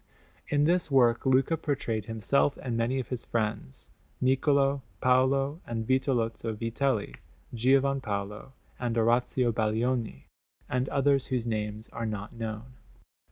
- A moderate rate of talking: No, slow, 125 wpm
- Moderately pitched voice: No, low, 125 Hz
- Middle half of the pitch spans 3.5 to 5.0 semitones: No, average, 3.1 semitones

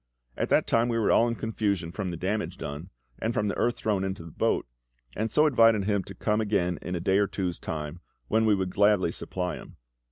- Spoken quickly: Yes, fast, 230 wpm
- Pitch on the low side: Yes, low, 100 Hz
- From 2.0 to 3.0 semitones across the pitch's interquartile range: No, average, 3.5 semitones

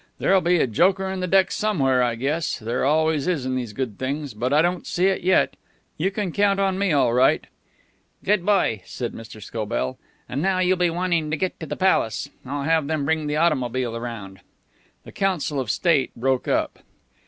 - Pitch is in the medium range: Yes, medium, 150 Hz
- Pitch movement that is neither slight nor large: No, wide, 6.3 semitones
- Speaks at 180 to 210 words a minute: Yes, average, 200 wpm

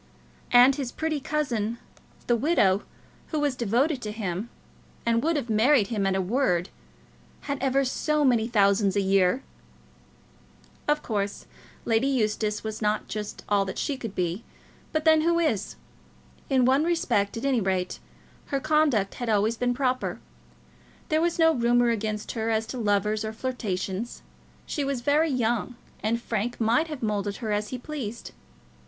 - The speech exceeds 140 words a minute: Yes, average, 160 wpm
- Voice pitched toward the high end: Yes, high, 235 Hz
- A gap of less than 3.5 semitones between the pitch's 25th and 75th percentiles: No, average, 4.7 semitones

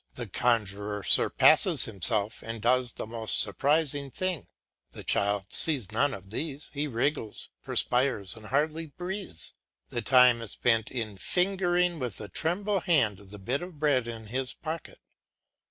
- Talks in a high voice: No, low, 125 Hz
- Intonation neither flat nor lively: No, wide, 6.1 semitones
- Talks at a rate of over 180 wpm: No, average, 150 wpm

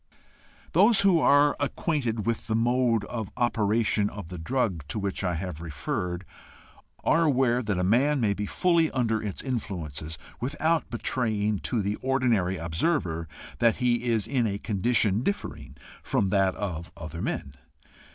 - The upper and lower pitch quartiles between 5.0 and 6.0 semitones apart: Yes, wide, 5.4 semitones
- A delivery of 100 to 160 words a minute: Yes, average, 150 wpm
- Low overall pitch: Yes, low, 110 Hz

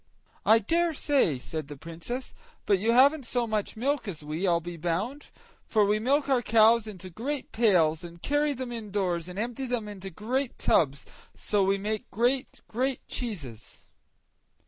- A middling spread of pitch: No, wide, 6.1 semitones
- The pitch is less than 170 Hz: No, high, 215 Hz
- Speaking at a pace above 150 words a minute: Yes, average, 170 wpm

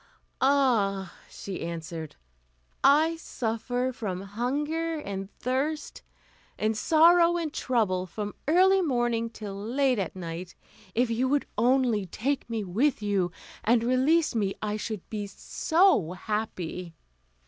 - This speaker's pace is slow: Yes, slow, 125 wpm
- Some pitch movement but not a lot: No, wide, 6.0 semitones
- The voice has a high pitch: Yes, high, 230 Hz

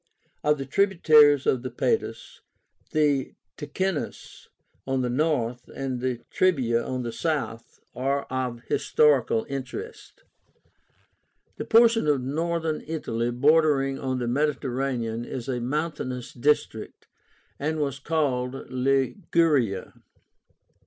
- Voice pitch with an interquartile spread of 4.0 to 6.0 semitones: No, average, 3.6 semitones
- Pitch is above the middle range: No, low, 135 Hz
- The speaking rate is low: Yes, slow, 110 wpm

